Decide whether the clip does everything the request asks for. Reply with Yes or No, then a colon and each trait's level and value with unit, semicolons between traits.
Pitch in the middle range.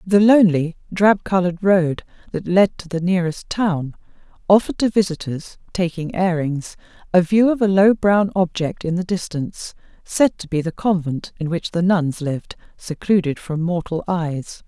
Yes: medium, 180 Hz